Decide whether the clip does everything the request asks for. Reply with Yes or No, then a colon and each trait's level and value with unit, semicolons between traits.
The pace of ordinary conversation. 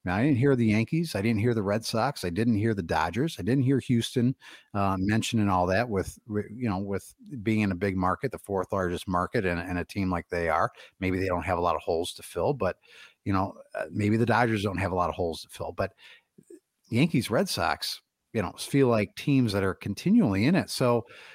No: fast, 235 wpm